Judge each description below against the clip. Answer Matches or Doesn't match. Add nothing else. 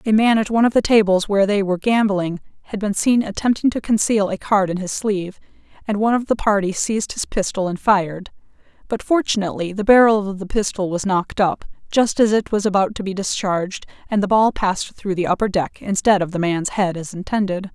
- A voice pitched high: Matches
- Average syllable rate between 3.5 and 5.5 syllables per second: Doesn't match